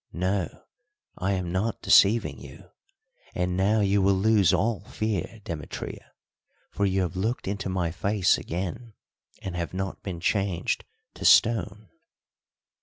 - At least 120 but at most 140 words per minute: Yes, slow, 135 wpm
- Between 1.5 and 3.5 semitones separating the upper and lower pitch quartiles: Yes, narrow, 2.5 semitones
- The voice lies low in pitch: Yes, very low, 95 Hz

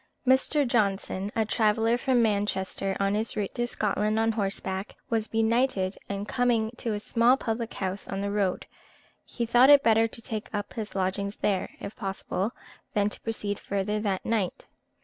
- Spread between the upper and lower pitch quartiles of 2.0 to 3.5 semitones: Yes, narrow, 2.6 semitones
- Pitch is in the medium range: No, high, 215 Hz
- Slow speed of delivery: No, average, 170 wpm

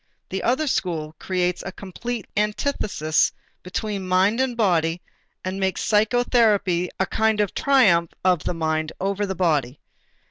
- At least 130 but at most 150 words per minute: Yes, average, 140 wpm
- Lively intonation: No, average, 3.9 semitones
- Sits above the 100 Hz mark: Yes, high, 190 Hz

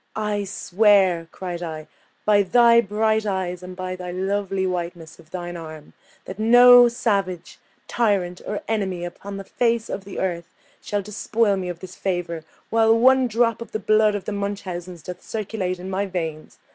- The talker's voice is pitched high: Yes, high, 195 Hz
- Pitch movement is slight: No, average, 3.4 semitones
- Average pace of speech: Yes, average, 170 wpm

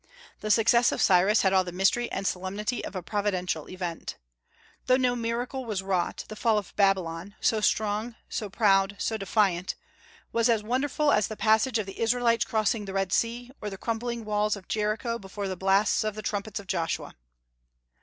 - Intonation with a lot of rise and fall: No, average, 3.0 semitones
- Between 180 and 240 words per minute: Yes, average, 185 wpm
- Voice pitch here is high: Yes, high, 210 Hz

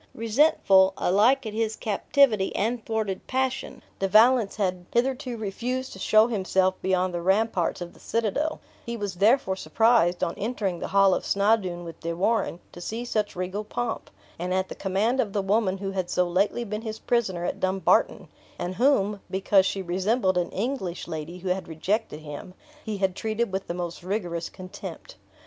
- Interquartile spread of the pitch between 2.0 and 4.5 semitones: Yes, average, 3.5 semitones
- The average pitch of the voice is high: Yes, high, 195 Hz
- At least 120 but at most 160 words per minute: No, average, 180 wpm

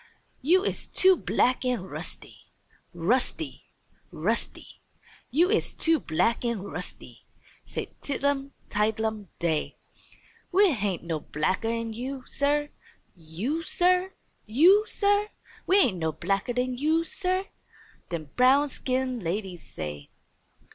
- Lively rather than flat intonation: Yes, wide, 8.7 semitones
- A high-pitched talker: Yes, very high, 250 Hz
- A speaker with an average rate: No, slow, 120 wpm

